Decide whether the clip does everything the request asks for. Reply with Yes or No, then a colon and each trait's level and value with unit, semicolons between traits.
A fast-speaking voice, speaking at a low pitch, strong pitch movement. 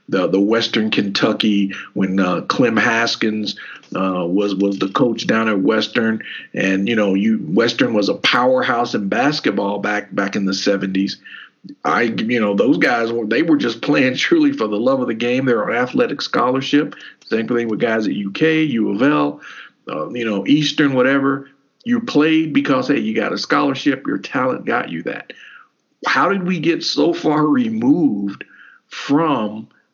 No: average, 175 wpm; low, 120 Hz; wide, 7.2 semitones